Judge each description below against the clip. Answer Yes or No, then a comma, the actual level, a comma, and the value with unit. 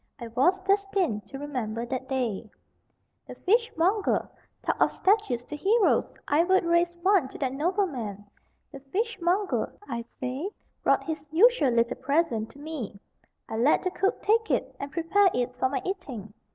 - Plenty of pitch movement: Yes, wide, 7.3 semitones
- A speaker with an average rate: Yes, average, 165 wpm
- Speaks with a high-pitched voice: Yes, very high, 300 Hz